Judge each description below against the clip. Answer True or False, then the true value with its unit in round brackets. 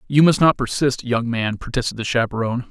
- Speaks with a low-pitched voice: True (125 Hz)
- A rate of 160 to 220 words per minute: True (200 wpm)